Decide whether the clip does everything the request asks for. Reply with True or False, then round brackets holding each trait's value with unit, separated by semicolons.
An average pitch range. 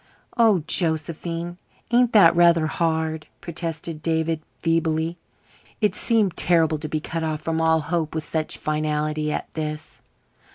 False (1.5 semitones)